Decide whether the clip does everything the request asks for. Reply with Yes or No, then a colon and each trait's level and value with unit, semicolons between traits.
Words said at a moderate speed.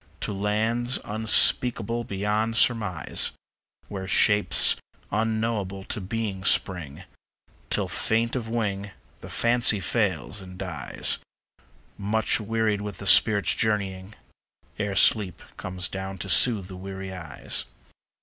No: slow, 115 wpm